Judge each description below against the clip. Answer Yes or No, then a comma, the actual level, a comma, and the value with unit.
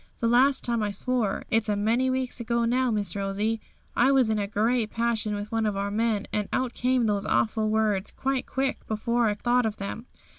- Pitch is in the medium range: No, high, 225 Hz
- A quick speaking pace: Yes, fast, 215 wpm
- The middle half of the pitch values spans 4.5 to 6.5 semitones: No, average, 2.7 semitones